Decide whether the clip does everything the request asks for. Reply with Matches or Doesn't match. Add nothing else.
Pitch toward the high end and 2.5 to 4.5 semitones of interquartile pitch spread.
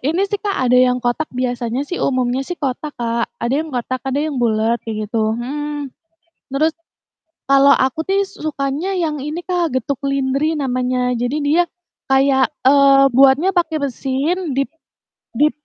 Matches